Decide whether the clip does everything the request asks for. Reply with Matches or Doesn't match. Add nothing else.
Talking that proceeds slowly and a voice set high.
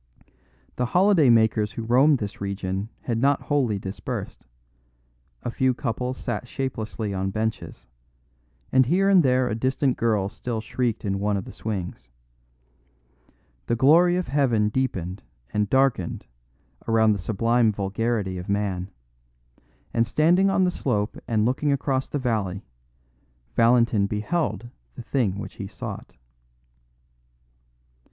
Doesn't match